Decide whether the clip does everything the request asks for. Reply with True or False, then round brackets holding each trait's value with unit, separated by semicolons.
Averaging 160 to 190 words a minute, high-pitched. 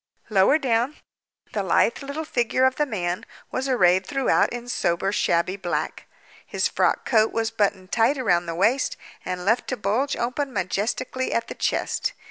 True (165 wpm; 225 Hz)